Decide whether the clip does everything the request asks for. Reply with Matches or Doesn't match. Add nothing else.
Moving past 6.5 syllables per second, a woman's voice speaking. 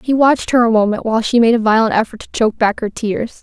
Matches